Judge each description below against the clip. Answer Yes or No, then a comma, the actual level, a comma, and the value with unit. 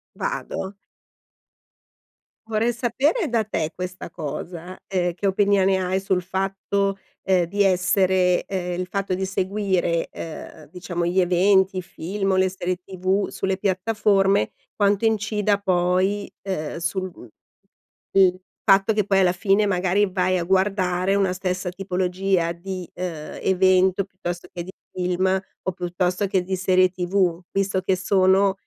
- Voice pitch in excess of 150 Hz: Yes, medium, 185 Hz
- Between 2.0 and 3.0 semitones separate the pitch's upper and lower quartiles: No, narrow, 1.5 semitones